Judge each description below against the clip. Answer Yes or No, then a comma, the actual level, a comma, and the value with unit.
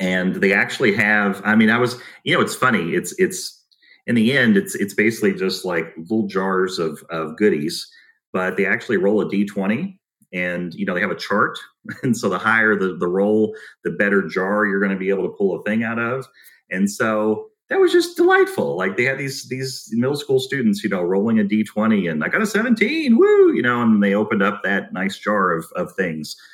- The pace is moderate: No, fast, 220 wpm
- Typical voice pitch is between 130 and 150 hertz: No, low, 110 Hz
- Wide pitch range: Yes, wide, 5.7 semitones